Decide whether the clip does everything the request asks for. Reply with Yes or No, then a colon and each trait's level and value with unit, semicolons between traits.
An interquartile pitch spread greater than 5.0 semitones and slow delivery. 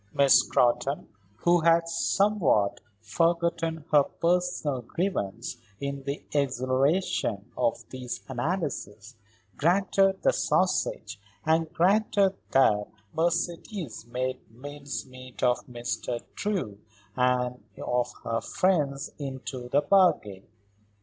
Yes: wide, 5.5 semitones; slow, 95 wpm